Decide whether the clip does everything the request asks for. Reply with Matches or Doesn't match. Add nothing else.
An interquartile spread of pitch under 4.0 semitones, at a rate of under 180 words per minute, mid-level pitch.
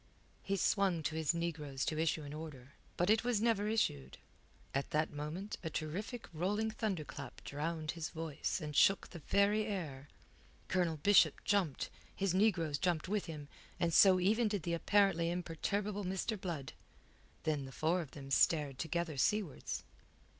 Doesn't match